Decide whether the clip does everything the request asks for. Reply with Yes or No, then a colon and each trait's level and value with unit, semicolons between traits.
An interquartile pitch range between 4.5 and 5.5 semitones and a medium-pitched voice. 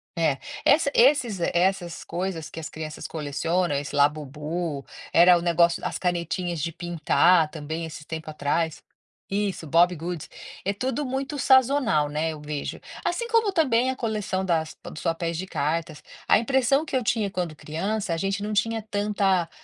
Yes: average, 5.2 semitones; medium, 175 Hz